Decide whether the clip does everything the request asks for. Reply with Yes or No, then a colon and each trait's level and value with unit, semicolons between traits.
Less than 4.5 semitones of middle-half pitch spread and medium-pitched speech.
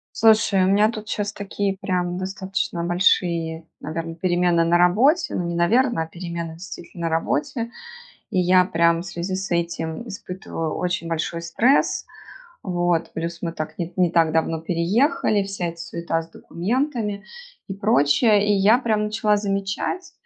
Yes: average, 3.5 semitones; medium, 180 Hz